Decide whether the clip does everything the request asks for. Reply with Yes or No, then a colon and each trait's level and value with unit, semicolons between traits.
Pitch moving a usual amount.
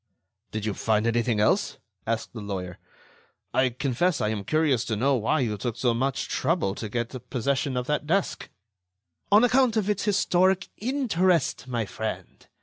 No: wide, 7.9 semitones